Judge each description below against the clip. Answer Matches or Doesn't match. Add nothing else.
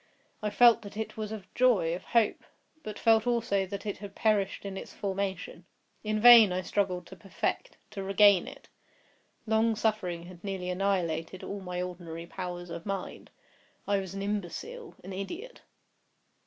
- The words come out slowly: Doesn't match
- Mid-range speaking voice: Doesn't match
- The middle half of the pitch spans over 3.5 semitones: Doesn't match